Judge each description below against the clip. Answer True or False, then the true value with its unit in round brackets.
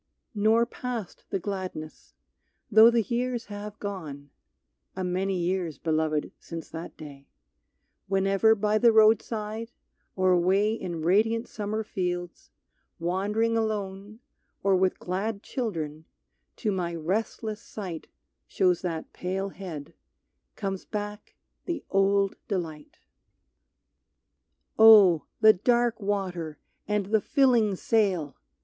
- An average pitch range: True (3.6 semitones)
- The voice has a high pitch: True (195 Hz)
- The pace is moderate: False (110 wpm)